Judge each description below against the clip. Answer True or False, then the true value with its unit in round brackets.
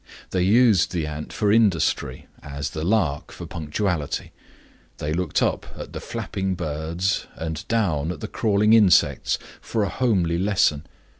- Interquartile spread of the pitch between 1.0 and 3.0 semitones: False (5.0 semitones)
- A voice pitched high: False (90 Hz)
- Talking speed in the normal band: True (150 wpm)